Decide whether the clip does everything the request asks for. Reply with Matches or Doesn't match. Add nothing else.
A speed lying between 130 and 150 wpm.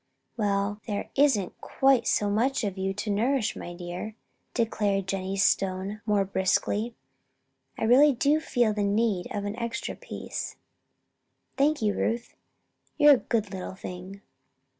Matches